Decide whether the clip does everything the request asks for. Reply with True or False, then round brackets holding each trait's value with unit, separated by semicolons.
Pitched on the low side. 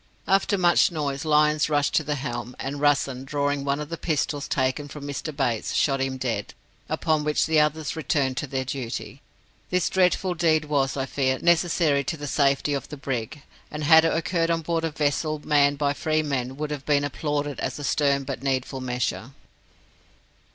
False (145 Hz)